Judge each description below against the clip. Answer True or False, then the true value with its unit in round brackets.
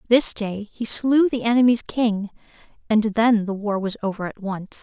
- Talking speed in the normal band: True (185 wpm)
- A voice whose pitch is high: True (220 Hz)